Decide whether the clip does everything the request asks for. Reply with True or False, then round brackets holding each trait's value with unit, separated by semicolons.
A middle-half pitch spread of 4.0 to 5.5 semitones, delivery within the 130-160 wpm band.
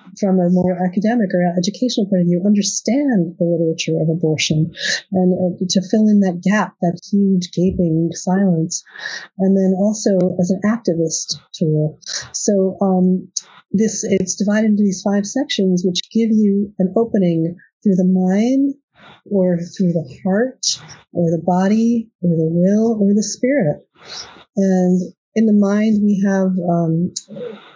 False (2.9 semitones; 150 wpm)